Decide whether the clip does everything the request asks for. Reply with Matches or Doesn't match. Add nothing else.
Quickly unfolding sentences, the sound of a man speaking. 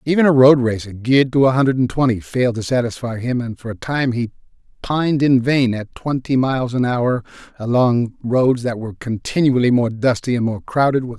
Matches